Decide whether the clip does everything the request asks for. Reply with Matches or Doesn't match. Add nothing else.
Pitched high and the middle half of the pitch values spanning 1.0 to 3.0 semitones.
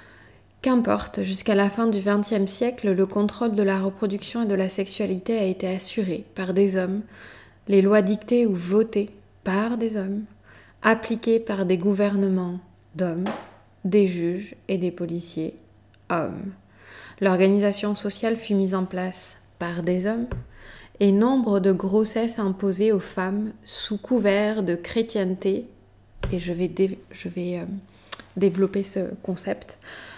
Matches